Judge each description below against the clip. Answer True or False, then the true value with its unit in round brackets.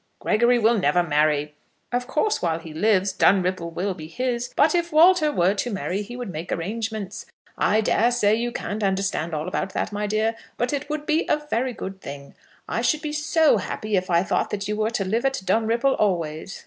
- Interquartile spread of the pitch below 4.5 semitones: False (5.1 semitones)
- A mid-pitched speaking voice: False (210 Hz)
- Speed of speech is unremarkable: False (210 wpm)